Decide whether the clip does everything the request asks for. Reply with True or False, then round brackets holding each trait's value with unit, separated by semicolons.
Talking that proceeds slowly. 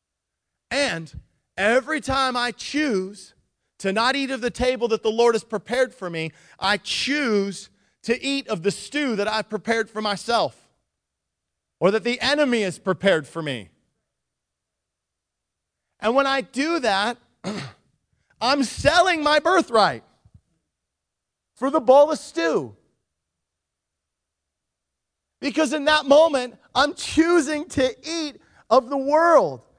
True (125 wpm)